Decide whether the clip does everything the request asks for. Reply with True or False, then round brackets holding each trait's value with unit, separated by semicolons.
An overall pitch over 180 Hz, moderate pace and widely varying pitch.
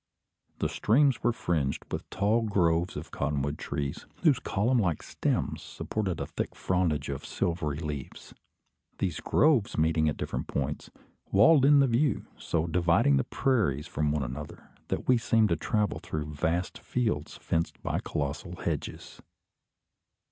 False (85 Hz; 150 wpm; 7.0 semitones)